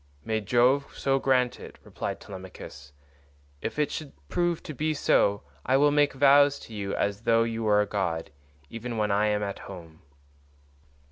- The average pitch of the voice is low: Yes, low, 115 Hz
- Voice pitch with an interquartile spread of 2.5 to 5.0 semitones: No, wide, 5.4 semitones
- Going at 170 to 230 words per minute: Yes, average, 175 wpm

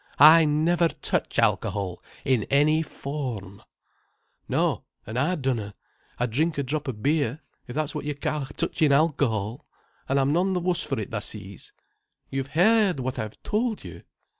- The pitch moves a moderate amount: Yes, average, 4.3 semitones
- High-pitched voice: No, medium, 145 Hz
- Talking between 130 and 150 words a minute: No, average, 165 wpm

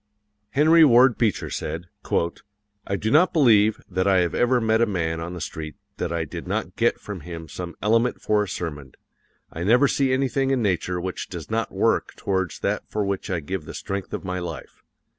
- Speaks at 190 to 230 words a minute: Yes, average, 200 wpm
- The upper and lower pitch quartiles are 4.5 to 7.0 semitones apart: Yes, average, 5.2 semitones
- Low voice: Yes, low, 100 Hz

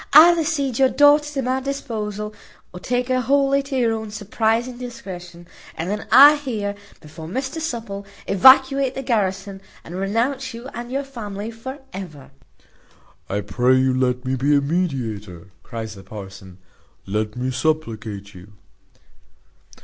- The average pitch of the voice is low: No, high, 210 Hz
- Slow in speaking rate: No, average, 150 wpm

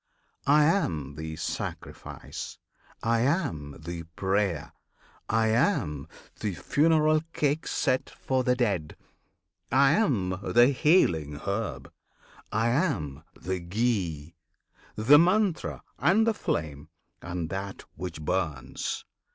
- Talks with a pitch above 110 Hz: No, low, 100 Hz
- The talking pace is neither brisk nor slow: No, slow, 110 wpm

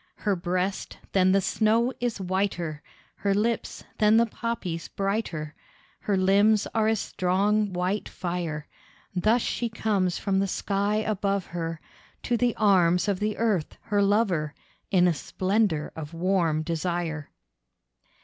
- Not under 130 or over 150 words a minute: Yes, average, 140 wpm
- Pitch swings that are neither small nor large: Yes, average, 3.4 semitones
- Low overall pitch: No, high, 195 Hz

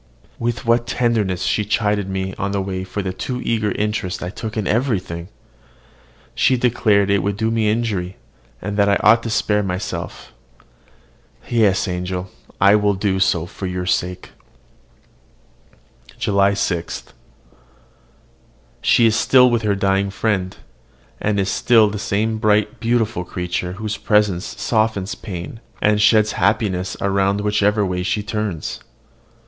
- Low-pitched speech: Yes, low, 100 Hz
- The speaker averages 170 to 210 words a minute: No, average, 145 wpm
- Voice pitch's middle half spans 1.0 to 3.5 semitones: Yes, narrow, 2.5 semitones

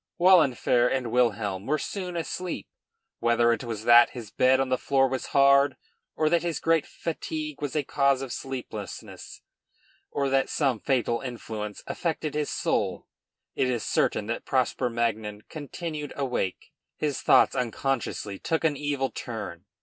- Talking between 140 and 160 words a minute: Yes, average, 150 wpm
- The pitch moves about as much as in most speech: Yes, average, 4.0 semitones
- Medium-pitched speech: No, low, 130 Hz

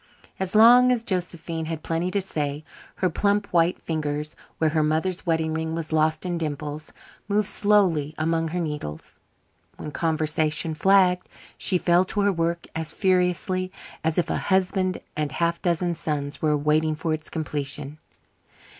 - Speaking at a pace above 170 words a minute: No, average, 160 wpm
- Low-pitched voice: No, medium, 165 Hz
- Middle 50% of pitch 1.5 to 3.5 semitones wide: Yes, average, 2.9 semitones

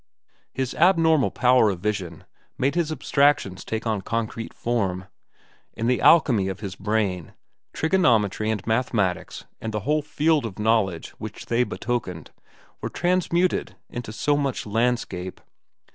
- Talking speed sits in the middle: No, slow, 130 wpm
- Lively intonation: Yes, wide, 5.8 semitones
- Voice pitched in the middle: No, low, 115 Hz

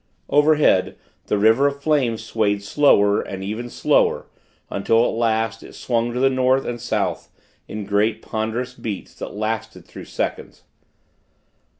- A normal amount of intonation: Yes, average, 3.4 semitones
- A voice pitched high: No, low, 115 Hz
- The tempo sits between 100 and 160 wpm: Yes, average, 140 wpm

